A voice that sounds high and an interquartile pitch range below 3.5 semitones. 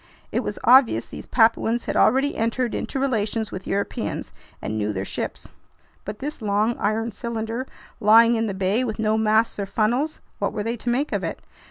Yes: high, 225 Hz; narrow, 2.5 semitones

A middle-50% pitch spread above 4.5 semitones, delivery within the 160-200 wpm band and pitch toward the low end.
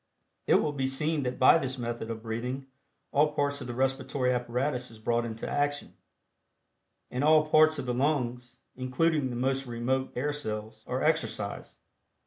No: average, 3.3 semitones; average, 165 wpm; low, 130 Hz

